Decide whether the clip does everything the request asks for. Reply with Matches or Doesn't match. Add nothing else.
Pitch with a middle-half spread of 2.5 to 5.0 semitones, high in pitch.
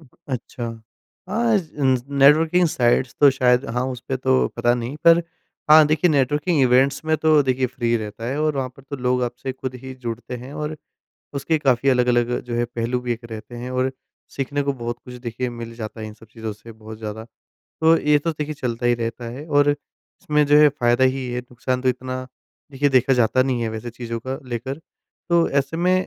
Doesn't match